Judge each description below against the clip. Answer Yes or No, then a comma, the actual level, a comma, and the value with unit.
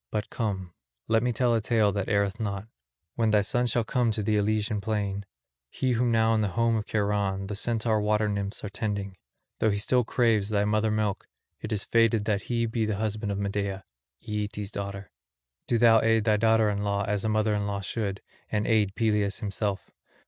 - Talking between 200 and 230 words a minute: Yes, fast, 205 wpm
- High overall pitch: No, low, 105 Hz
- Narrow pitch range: Yes, narrow, 1.7 semitones